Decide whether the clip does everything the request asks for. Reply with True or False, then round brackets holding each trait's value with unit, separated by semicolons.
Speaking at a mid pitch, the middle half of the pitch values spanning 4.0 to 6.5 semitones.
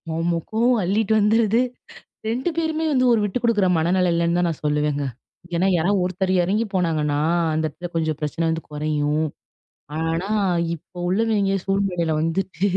True (180 Hz; 4.4 semitones)